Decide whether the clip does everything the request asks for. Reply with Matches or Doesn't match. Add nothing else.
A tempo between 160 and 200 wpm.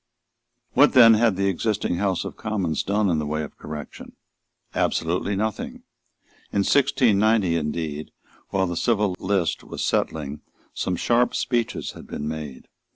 Doesn't match